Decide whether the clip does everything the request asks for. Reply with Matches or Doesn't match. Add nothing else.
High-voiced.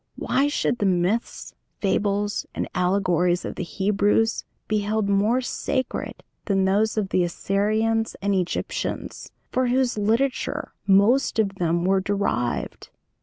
Matches